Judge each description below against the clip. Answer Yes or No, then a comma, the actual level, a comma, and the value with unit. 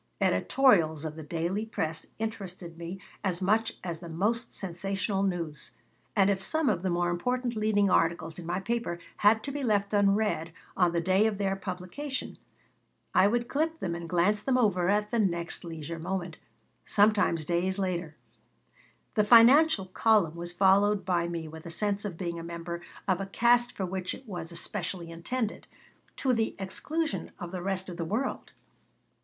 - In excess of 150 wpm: Yes, average, 175 wpm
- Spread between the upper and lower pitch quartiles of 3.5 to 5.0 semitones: Yes, average, 4.0 semitones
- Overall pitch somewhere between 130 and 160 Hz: No, high, 190 Hz